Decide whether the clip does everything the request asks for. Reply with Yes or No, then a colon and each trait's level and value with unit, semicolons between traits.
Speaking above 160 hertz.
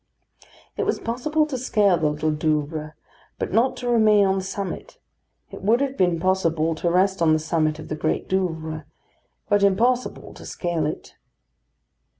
Yes: medium, 185 Hz